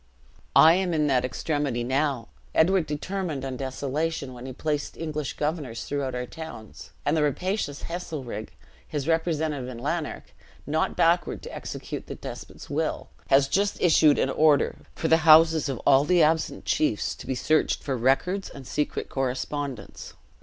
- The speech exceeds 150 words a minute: Yes, average, 160 wpm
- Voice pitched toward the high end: No, medium, 150 Hz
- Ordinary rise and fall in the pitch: Yes, average, 3.4 semitones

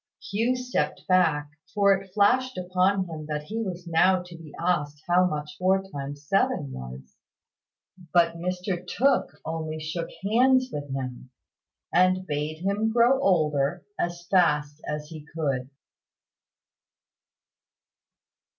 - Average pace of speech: No, slow, 125 wpm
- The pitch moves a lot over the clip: No, average, 4.6 semitones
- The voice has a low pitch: No, medium, 175 Hz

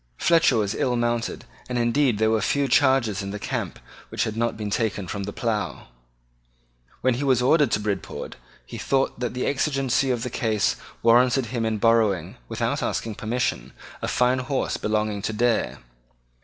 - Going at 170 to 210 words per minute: Yes, average, 175 wpm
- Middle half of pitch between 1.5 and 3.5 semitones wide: Yes, average, 3.1 semitones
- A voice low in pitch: Yes, low, 115 Hz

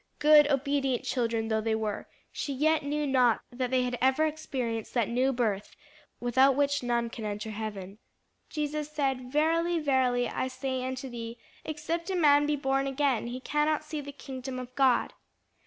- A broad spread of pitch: No, average, 3.3 semitones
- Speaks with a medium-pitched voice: No, very high, 260 Hz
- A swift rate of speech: No, average, 170 wpm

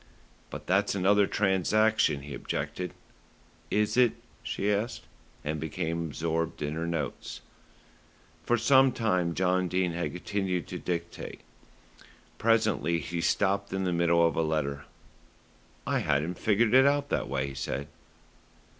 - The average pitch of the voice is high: No, very low, 90 Hz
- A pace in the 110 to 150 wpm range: Yes, slow, 135 wpm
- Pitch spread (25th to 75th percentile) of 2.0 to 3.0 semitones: No, average, 4.1 semitones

